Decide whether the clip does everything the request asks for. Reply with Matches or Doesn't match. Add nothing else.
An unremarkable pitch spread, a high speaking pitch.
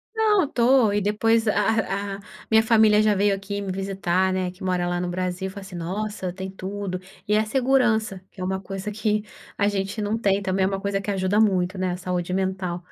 Doesn't match